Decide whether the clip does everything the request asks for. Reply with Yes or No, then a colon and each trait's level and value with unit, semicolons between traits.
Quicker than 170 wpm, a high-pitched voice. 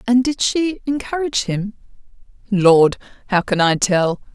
No: average, 140 wpm; high, 220 Hz